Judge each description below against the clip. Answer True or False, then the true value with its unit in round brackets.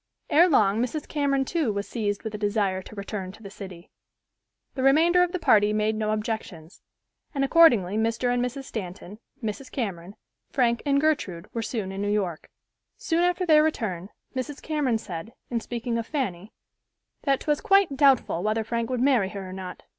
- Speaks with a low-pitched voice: False (225 Hz)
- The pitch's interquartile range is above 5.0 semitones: True (5.5 semitones)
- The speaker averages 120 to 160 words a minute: False (185 wpm)